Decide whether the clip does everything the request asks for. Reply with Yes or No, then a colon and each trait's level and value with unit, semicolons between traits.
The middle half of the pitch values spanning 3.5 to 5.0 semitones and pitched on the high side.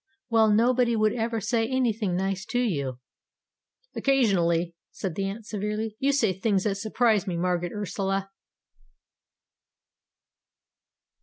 No: average, 3.1 semitones; high, 210 Hz